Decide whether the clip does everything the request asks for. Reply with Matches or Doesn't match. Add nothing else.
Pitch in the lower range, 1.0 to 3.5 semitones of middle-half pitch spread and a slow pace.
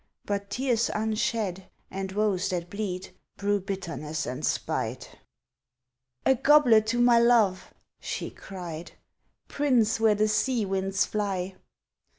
Doesn't match